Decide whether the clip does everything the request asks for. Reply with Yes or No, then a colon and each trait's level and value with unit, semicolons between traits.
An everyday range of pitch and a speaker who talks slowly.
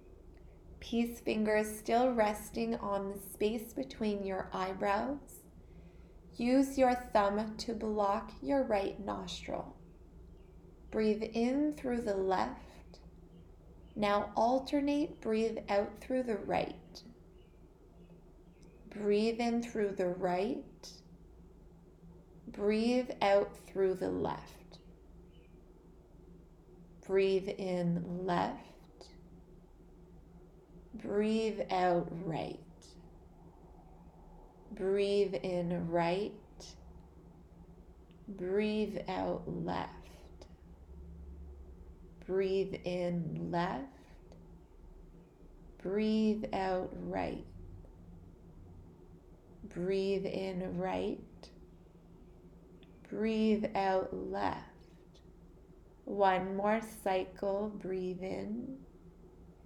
Yes: average, 3.5 semitones; slow, 70 wpm